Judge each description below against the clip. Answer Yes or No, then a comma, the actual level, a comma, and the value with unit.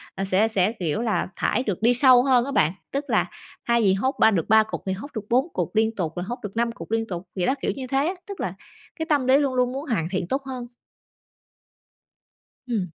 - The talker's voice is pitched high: Yes, high, 230 Hz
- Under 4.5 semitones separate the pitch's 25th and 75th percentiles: No, average, 5.1 semitones